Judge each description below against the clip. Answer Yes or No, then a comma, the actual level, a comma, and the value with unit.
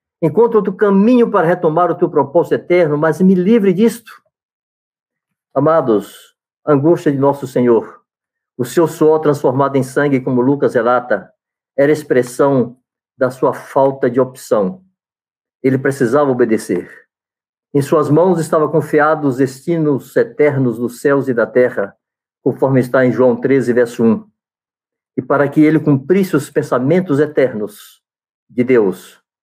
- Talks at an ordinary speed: Yes, average, 140 wpm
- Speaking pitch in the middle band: Yes, medium, 145 Hz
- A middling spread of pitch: Yes, average, 4.6 semitones